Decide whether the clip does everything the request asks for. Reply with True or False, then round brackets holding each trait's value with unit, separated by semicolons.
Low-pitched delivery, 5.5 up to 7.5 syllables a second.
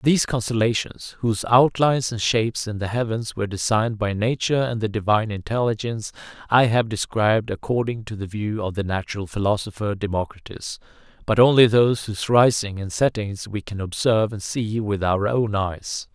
True (110 Hz; 5.6 syllables/s)